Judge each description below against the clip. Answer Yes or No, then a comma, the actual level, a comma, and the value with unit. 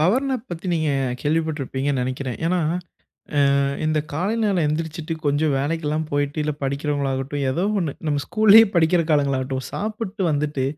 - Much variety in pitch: No, average, 3.3 semitones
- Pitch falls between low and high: Yes, medium, 150 Hz